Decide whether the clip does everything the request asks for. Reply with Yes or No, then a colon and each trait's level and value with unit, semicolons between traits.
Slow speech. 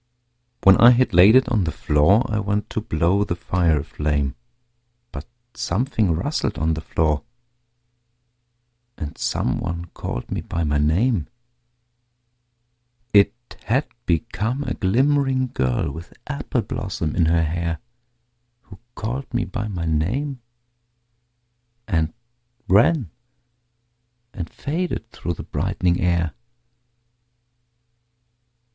Yes: slow, 115 wpm